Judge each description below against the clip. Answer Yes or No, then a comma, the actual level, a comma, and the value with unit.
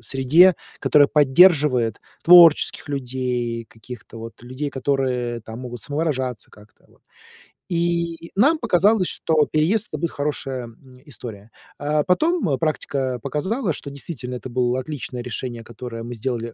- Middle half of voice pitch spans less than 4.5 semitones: No, average, 4.8 semitones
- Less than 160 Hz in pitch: Yes, low, 135 Hz